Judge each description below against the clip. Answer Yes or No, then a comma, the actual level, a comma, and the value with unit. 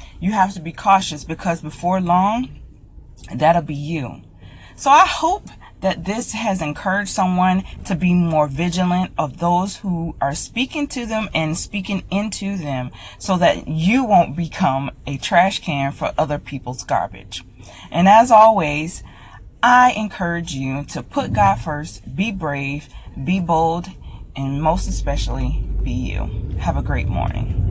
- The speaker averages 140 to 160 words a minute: Yes, average, 150 wpm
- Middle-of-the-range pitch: Yes, medium, 165 Hz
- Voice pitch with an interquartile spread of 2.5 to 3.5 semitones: No, wide, 5.5 semitones